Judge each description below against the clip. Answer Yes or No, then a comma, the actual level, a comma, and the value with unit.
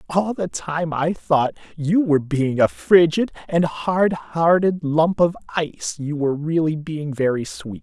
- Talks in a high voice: No, medium, 160 Hz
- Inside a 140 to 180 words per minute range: Yes, average, 170 wpm